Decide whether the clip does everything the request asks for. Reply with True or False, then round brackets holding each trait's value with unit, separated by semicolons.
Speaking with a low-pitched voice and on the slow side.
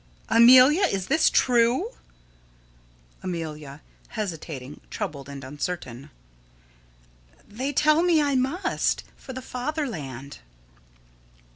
False (230 Hz; 90 wpm)